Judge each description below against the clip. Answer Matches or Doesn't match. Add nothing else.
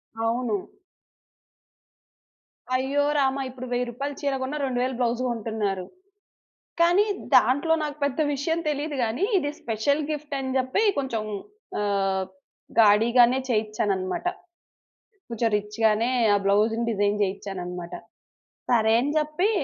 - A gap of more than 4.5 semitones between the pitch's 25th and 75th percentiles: Matches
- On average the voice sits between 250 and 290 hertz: Doesn't match